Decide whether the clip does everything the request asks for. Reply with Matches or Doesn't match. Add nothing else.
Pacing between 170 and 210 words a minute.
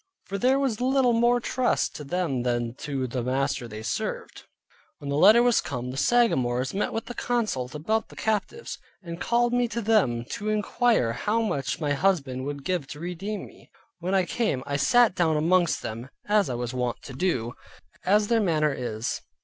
Matches